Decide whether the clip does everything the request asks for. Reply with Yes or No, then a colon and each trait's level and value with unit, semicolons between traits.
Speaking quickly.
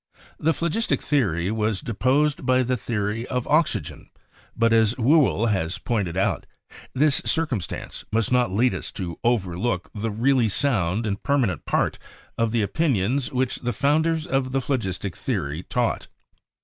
No: average, 150 wpm